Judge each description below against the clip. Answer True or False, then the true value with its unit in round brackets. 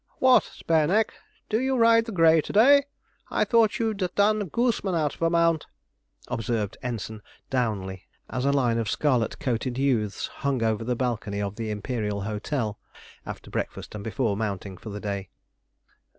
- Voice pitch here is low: True (125 Hz)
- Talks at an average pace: True (165 wpm)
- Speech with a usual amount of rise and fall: False (7.9 semitones)